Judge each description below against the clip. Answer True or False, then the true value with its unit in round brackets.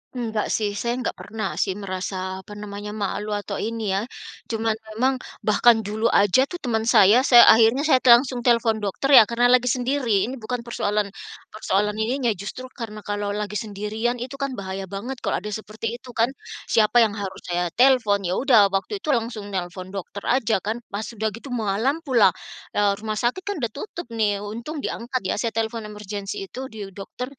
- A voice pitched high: True (220 Hz)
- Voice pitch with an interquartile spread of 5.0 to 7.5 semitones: False (3.1 semitones)